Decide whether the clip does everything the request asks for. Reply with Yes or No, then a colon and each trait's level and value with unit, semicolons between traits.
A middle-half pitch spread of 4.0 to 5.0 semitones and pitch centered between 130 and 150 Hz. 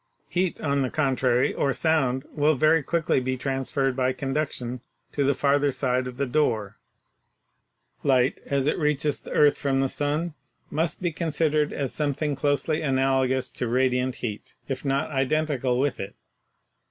No: narrow, 2.6 semitones; medium, 140 Hz